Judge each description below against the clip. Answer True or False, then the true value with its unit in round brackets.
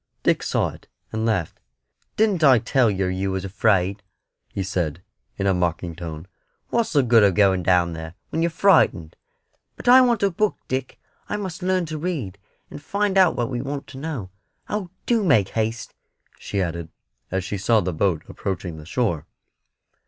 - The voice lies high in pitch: False (110 Hz)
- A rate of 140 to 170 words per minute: False (180 wpm)